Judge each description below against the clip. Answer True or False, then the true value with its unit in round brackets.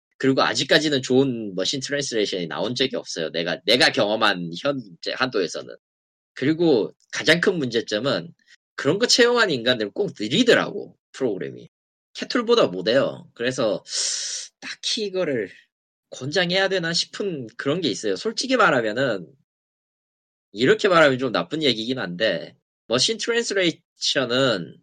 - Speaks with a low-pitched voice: False (170 Hz)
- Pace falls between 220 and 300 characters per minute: False (310 characters per minute)